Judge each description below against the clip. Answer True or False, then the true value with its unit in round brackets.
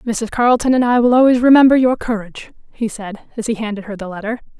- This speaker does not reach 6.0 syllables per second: False (6.5 syllables/s)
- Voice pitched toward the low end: False (230 Hz)